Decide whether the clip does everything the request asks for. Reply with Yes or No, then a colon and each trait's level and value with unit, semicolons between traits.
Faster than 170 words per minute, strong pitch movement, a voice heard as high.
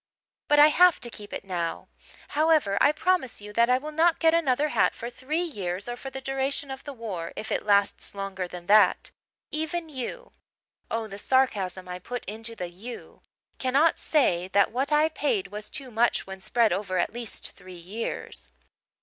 Yes: average, 190 wpm; wide, 6.8 semitones; high, 235 Hz